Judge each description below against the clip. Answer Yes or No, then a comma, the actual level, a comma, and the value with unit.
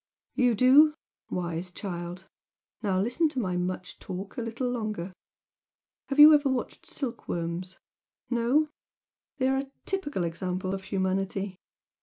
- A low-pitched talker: No, high, 200 Hz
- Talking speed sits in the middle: No, slow, 125 wpm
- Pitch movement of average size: No, wide, 6.1 semitones